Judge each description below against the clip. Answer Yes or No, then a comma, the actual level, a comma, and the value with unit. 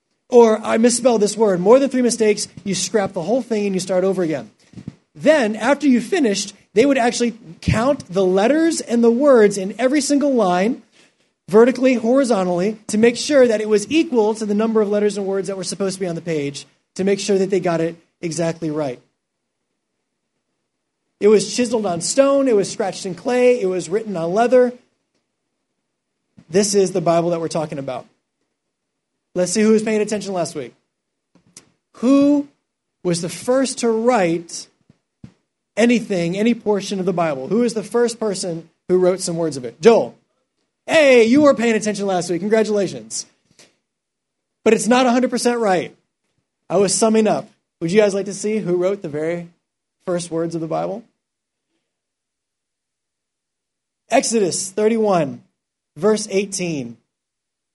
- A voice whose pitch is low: No, high, 210 Hz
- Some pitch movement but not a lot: Yes, average, 4.7 semitones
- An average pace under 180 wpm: Yes, average, 165 wpm